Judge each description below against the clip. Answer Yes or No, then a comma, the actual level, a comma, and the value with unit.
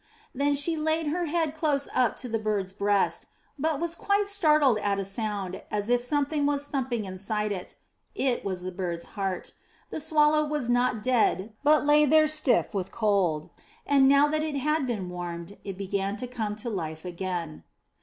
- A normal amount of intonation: No, wide, 7.2 semitones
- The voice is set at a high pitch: Yes, high, 245 Hz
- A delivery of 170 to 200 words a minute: Yes, average, 185 wpm